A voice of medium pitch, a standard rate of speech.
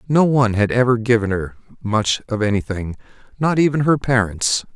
No: low, 115 Hz; average, 150 wpm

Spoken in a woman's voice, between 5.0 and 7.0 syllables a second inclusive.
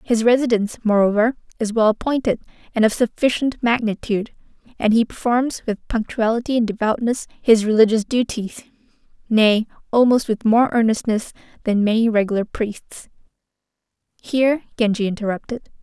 Yes: female; 5.3 syllables/s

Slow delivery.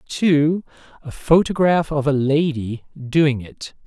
Yes: slow, 125 wpm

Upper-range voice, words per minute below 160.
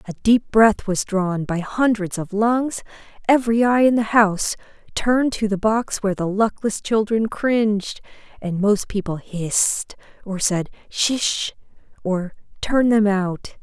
Yes: high, 210 Hz; average, 150 wpm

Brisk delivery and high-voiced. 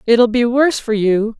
Yes: fast, 215 wpm; high, 230 Hz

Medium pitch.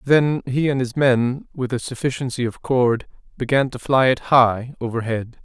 No: low, 125 Hz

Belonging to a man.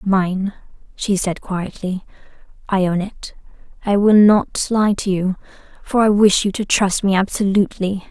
No: female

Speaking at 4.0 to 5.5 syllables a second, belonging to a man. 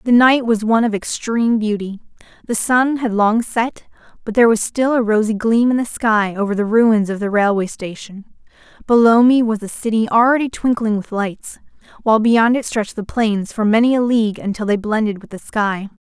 No: 5.3 syllables/s; female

